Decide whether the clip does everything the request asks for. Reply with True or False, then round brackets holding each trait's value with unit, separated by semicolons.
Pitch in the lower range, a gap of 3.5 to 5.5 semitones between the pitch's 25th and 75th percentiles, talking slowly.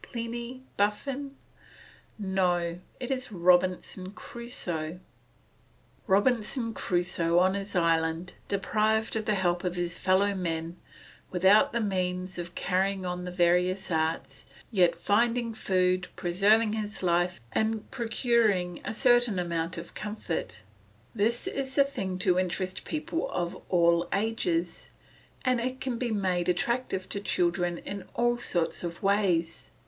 False (190 Hz; 4.2 semitones; 130 wpm)